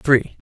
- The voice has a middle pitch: No, low, 125 Hz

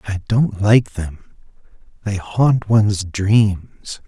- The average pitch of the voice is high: No, low, 100 Hz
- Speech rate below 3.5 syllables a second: Yes, 3.0 syllables/s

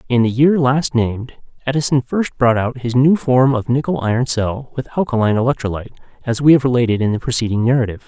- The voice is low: Yes, low, 125 Hz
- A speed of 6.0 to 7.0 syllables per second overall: Yes, 6.4 syllables/s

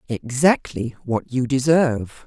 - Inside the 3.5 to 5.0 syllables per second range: Yes, 4.3 syllables/s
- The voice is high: No, low, 130 Hz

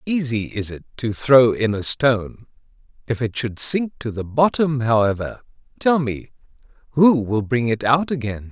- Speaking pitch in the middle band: No, low, 125 Hz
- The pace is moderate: Yes, average, 170 wpm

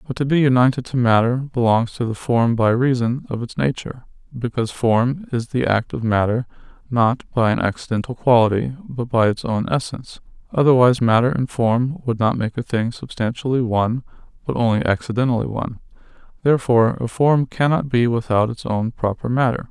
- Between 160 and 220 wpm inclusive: Yes, average, 175 wpm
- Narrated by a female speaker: No, male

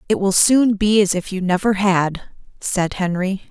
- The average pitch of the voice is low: No, high, 195 Hz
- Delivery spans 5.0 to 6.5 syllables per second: No, 4.5 syllables/s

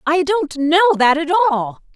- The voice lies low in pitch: No, very high, 320 Hz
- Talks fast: No, average, 185 wpm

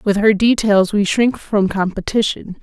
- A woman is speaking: Yes, female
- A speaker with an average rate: Yes, average, 160 wpm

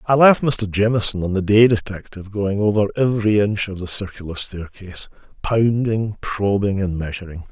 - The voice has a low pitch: Yes, low, 105 Hz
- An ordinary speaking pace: Yes, average, 160 wpm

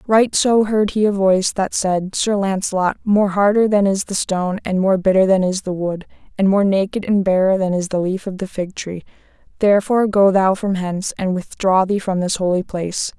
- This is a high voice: Yes, high, 195 Hz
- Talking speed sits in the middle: No, fast, 220 wpm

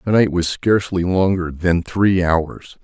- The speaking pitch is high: No, very low, 90 Hz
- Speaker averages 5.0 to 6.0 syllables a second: No, 4.1 syllables/s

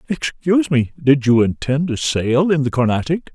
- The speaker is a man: Yes, male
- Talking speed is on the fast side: No, average, 180 wpm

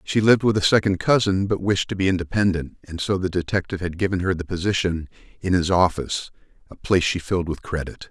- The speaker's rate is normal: No, fast, 215 wpm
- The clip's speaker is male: Yes, male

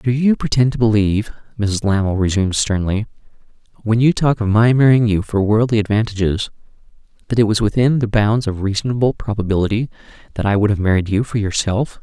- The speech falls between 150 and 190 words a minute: Yes, average, 180 wpm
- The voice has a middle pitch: No, low, 110 Hz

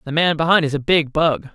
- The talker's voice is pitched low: No, medium, 150 Hz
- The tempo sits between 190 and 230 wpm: No, fast, 270 wpm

